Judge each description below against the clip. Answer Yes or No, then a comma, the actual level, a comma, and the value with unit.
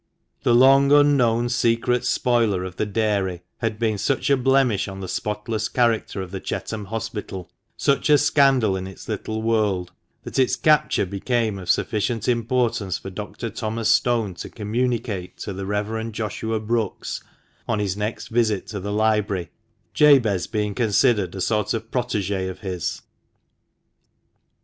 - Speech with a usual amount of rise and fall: Yes, average, 3.1 semitones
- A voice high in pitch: No, low, 110 Hz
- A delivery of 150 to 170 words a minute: Yes, average, 155 wpm